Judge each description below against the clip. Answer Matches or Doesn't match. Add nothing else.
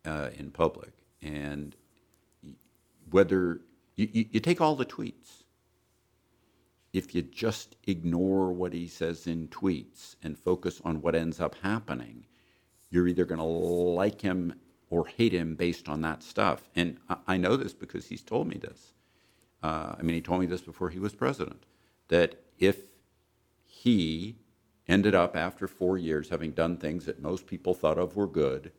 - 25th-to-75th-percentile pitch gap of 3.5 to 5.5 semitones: Doesn't match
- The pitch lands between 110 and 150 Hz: Doesn't match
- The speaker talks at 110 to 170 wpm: Matches